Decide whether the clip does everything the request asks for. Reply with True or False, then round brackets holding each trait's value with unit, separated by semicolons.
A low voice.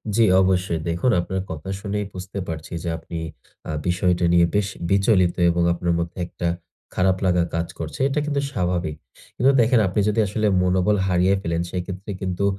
True (90 Hz)